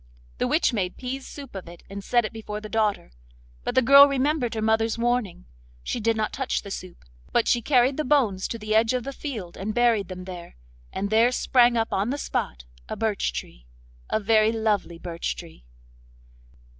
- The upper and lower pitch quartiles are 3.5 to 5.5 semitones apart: Yes, average, 4.1 semitones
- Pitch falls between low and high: No, high, 220 Hz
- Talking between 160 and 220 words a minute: Yes, average, 195 wpm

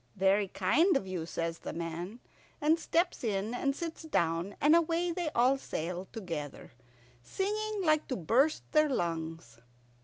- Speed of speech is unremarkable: Yes, average, 150 wpm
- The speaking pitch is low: No, high, 225 Hz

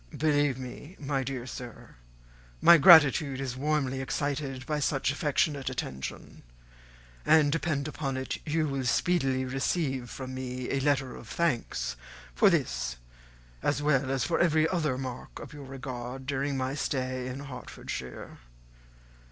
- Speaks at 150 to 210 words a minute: No, average, 140 wpm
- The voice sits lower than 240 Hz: Yes, low, 135 Hz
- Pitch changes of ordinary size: No, narrow, 2.3 semitones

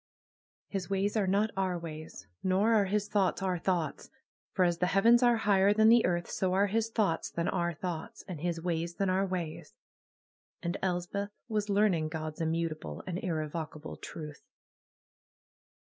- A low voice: No, medium, 185 Hz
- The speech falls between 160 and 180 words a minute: Yes, average, 165 wpm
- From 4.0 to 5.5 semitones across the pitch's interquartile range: No, average, 3.3 semitones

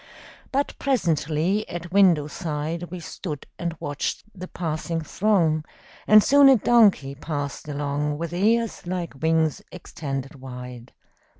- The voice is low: No, medium, 165 Hz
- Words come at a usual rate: No, slow, 125 wpm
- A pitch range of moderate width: Yes, average, 4.3 semitones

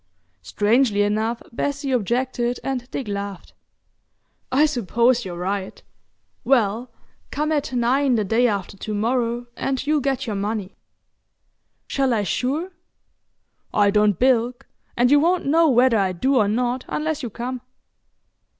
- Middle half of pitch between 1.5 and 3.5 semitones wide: No, average, 4.2 semitones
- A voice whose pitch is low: No, high, 245 Hz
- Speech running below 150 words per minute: Yes, average, 140 wpm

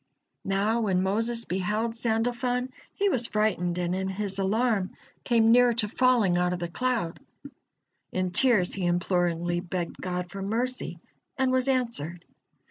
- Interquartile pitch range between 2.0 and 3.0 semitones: No, average, 4.9 semitones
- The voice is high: Yes, high, 205 Hz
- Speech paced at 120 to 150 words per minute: Yes, average, 145 wpm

